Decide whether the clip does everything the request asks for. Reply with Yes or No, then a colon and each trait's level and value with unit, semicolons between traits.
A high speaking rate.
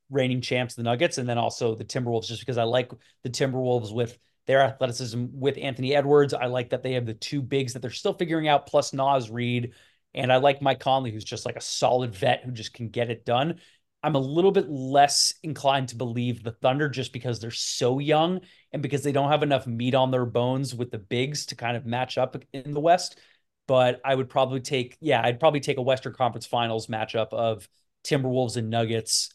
Yes: fast, 220 wpm